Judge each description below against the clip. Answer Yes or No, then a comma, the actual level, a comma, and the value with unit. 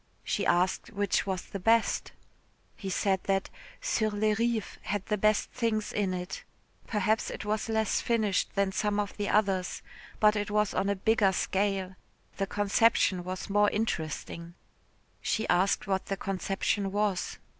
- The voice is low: No, high, 205 Hz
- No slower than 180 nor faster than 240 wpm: No, average, 155 wpm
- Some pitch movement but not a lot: No, narrow, 1.9 semitones